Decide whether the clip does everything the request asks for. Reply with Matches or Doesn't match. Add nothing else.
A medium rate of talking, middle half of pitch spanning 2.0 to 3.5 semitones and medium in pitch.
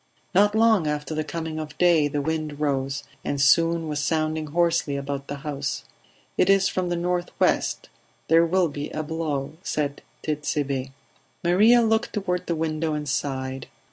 Matches